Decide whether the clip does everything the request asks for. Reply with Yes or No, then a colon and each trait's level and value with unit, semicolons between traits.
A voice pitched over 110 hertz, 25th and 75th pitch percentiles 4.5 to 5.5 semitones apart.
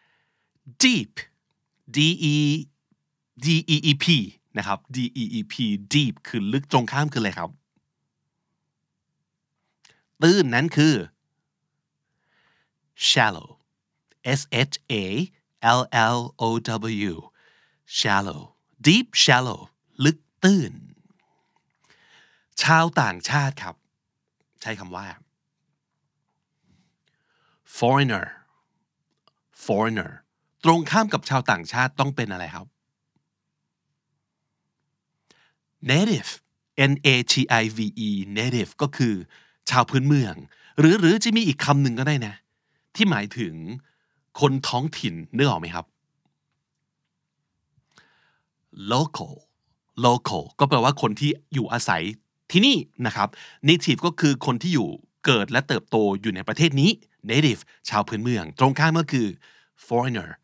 Yes: medium, 140 Hz; average, 5.1 semitones